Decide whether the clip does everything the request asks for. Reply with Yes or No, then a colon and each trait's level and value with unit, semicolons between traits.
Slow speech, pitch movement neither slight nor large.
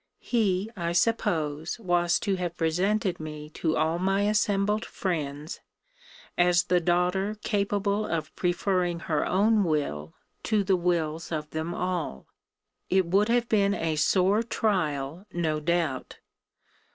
Yes: slow, 130 wpm; average, 3.9 semitones